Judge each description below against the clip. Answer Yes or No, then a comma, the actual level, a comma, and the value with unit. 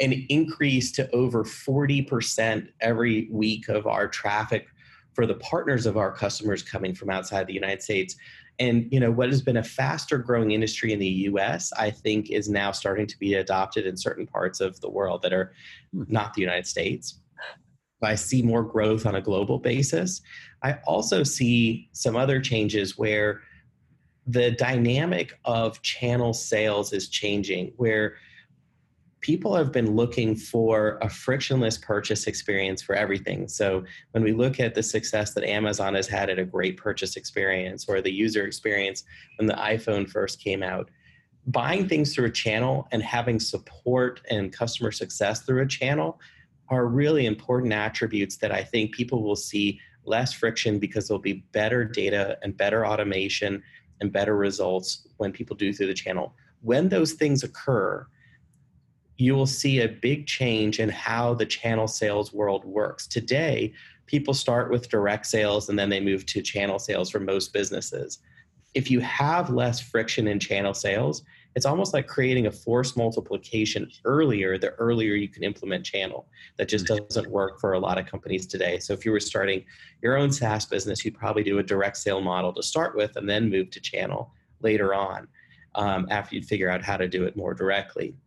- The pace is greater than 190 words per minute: No, average, 175 wpm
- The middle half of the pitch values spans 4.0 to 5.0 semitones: No, average, 3.6 semitones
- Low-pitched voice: Yes, low, 110 Hz